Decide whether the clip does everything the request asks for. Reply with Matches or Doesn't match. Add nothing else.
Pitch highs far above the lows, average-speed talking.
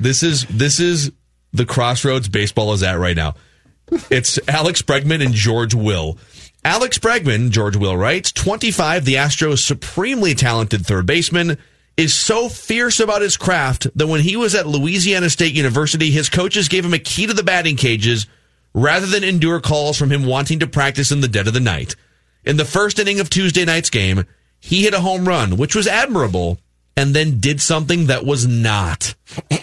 Matches